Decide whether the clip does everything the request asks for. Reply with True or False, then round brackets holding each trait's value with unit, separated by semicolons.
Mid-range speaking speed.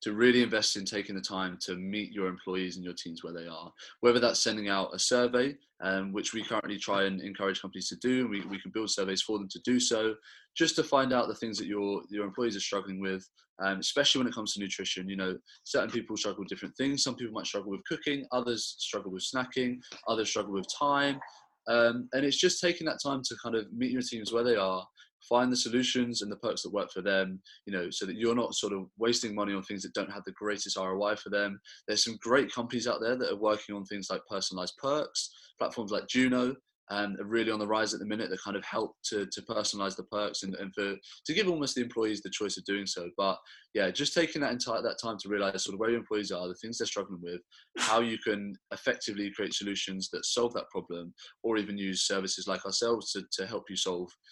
False (245 wpm)